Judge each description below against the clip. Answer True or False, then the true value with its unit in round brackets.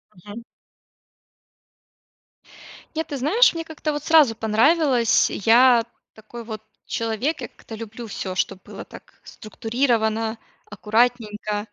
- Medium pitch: False (230 Hz)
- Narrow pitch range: False (3.6 semitones)